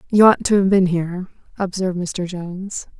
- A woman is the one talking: Yes, female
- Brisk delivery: No, average, 180 wpm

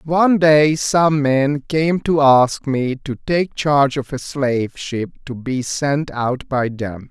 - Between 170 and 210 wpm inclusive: Yes, average, 175 wpm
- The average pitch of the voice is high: No, medium, 140 Hz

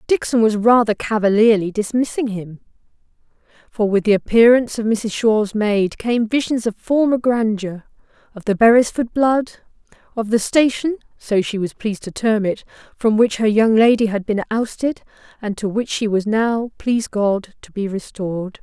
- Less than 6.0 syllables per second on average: Yes, 4.5 syllables/s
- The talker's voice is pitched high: Yes, high, 220 Hz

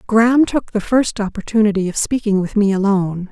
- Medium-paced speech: Yes, average, 180 wpm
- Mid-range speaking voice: No, high, 210 Hz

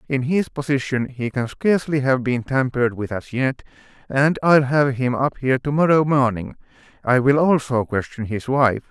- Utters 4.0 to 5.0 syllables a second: Yes, 4.9 syllables/s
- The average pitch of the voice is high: No, low, 130 Hz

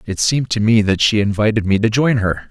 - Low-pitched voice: Yes, low, 110 Hz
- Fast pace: Yes, fast, 265 wpm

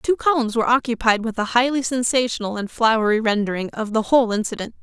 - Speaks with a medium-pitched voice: No, high, 230 Hz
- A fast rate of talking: No, average, 185 wpm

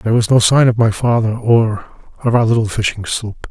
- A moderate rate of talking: No, fast, 240 wpm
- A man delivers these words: Yes, male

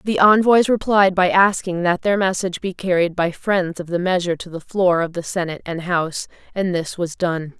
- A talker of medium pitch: Yes, medium, 180 Hz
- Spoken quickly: Yes, fast, 215 wpm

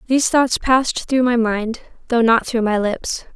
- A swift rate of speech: No, average, 195 wpm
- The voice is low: No, high, 235 Hz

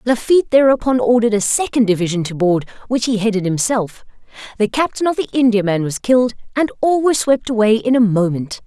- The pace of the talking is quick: No, average, 185 wpm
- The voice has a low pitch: No, high, 230 Hz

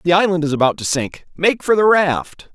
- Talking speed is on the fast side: Yes, fast, 235 wpm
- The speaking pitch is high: No, medium, 165 Hz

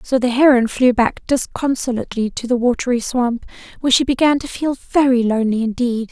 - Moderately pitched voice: No, high, 245 Hz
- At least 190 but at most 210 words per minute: No, average, 175 wpm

